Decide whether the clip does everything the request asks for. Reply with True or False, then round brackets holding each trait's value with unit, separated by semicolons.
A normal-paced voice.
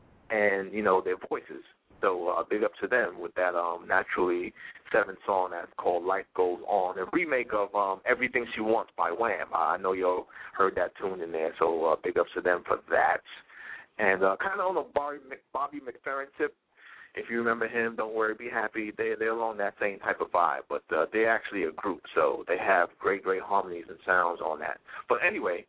False (215 wpm)